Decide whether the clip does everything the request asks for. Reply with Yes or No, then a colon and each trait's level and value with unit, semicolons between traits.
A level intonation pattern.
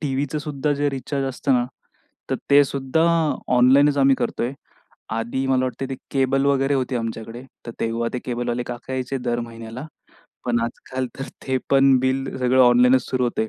Yes: narrow, 2.0 semitones